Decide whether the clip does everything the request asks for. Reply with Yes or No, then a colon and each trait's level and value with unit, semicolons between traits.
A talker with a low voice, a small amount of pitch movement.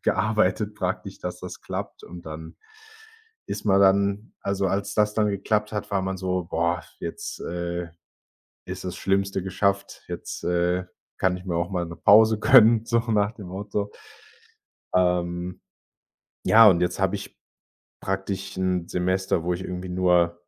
Yes: very low, 95 Hz; narrow, 2.3 semitones